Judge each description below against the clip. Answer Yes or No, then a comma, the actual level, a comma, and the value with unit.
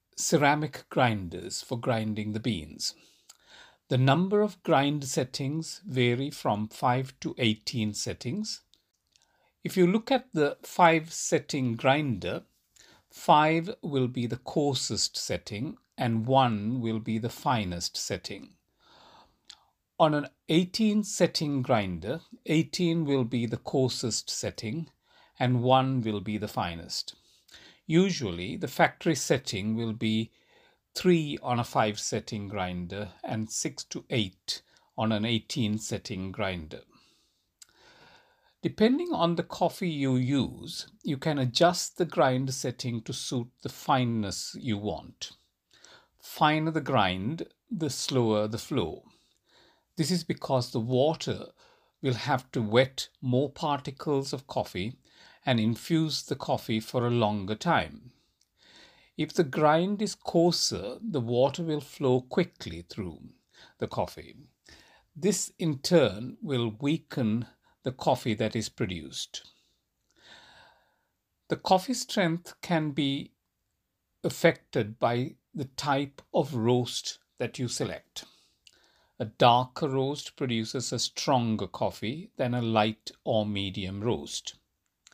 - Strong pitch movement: Yes, wide, 6.1 semitones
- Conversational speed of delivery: No, slow, 120 wpm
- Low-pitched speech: Yes, low, 130 Hz